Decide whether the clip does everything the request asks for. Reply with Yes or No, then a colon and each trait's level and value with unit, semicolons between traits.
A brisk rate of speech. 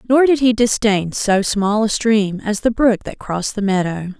Yes: fast, 215 wpm